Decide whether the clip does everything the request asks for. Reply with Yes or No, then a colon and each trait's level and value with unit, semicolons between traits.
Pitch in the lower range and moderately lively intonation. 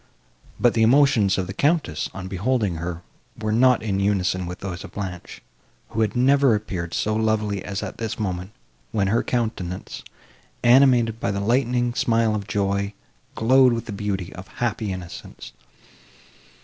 Yes: low, 105 Hz; average, 3.8 semitones